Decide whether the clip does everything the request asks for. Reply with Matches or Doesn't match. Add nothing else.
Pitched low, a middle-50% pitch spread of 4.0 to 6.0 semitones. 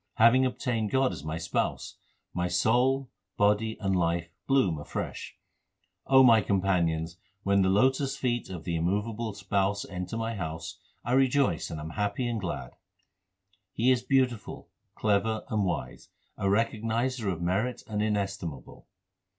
Matches